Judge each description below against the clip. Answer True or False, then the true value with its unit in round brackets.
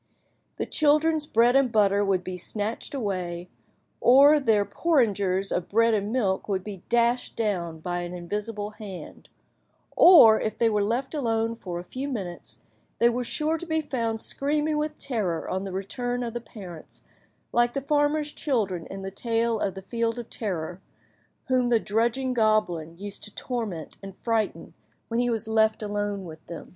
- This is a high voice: True (220 Hz)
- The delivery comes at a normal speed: True (175 wpm)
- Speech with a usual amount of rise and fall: True (4.2 semitones)